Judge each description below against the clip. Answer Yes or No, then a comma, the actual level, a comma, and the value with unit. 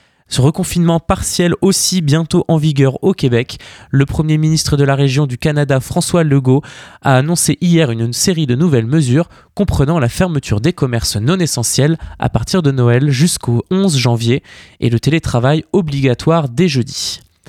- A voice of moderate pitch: Yes, medium, 145 Hz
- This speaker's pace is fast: No, average, 160 wpm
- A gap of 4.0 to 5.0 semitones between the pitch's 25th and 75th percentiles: Yes, average, 4.7 semitones